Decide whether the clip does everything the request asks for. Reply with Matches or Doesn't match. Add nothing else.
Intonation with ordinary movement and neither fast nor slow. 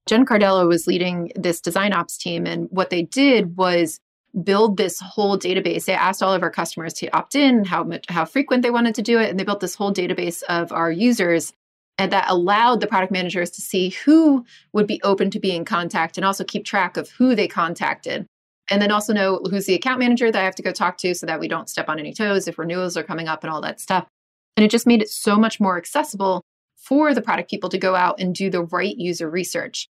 Doesn't match